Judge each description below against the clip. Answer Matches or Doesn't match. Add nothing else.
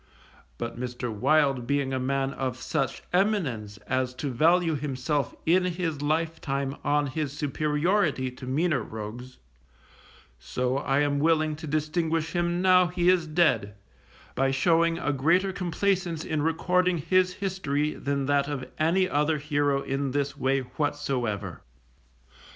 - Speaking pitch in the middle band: Matches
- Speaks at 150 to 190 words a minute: Doesn't match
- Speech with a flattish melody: Doesn't match